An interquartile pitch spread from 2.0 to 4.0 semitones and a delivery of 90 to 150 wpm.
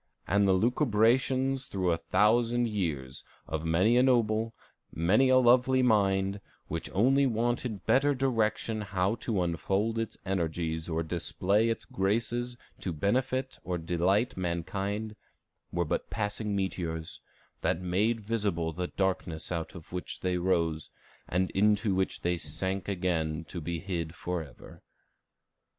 No: average, 4.7 semitones; slow, 135 wpm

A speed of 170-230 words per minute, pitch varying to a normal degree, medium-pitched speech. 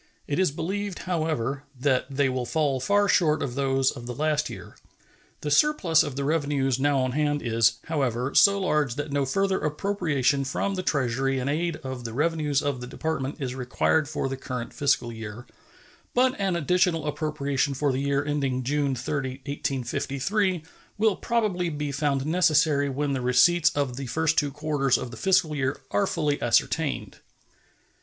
Yes: average, 175 wpm; average, 3.3 semitones; medium, 145 Hz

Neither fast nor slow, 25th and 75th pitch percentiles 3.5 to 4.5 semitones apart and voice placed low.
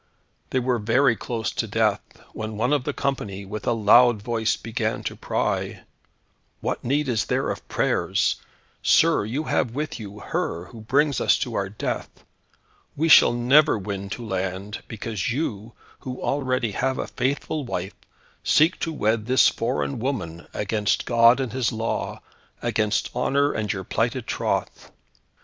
Yes: average, 160 wpm; average, 3.9 semitones; low, 115 Hz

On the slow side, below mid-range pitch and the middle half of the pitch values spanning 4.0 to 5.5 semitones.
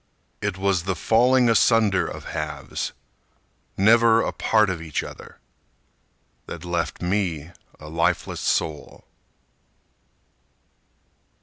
Yes: slow, 100 wpm; very low, 95 Hz; average, 5.2 semitones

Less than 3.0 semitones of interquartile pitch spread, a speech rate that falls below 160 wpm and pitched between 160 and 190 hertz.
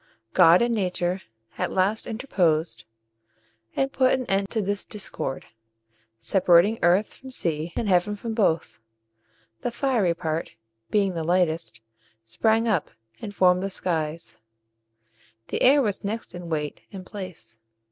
No: average, 4.5 semitones; slow, 135 wpm; medium, 185 Hz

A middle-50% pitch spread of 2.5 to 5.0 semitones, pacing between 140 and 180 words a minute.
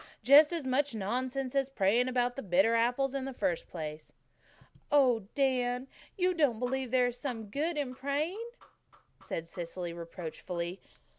No: wide, 5.6 semitones; average, 150 wpm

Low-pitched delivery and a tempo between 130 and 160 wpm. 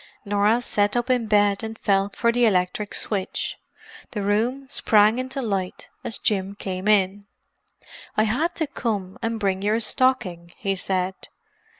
No: high, 210 Hz; average, 155 wpm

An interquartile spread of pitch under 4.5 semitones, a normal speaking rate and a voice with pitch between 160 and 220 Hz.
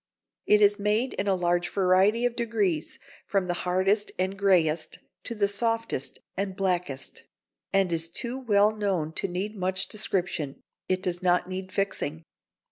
Yes: average, 2.7 semitones; average, 155 wpm; high, 190 Hz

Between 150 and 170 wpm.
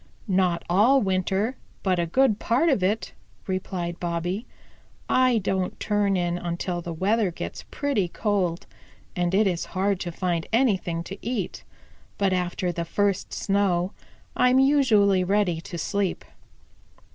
No: average, 140 wpm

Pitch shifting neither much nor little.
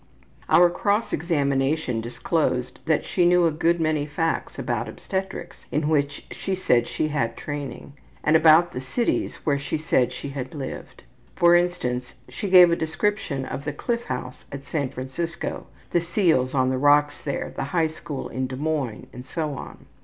Yes: average, 4.1 semitones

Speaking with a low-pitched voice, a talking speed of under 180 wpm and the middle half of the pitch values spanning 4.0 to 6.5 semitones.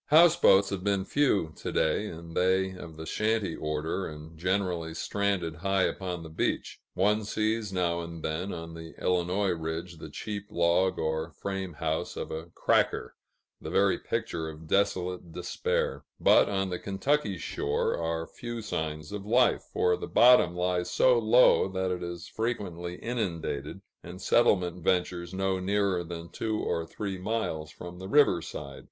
No: very low, 90 Hz; average, 160 wpm; average, 3.4 semitones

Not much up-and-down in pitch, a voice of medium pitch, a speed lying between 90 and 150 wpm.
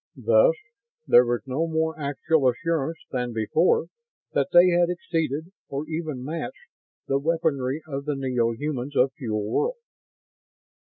No: average, 4.3 semitones; medium, 150 Hz; average, 140 wpm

